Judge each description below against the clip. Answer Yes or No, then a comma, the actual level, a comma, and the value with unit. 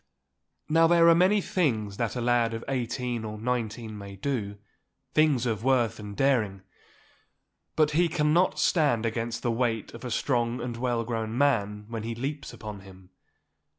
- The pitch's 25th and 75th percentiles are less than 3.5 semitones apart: No, average, 3.8 semitones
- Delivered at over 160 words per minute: No, average, 155 wpm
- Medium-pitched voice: No, low, 120 Hz